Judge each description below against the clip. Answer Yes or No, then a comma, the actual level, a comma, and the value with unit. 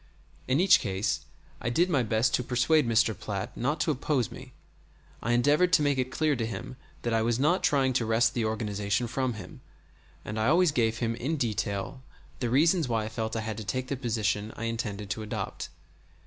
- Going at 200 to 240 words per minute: Yes, fast, 205 wpm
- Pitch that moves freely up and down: No, average, 3.6 semitones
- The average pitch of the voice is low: Yes, low, 120 Hz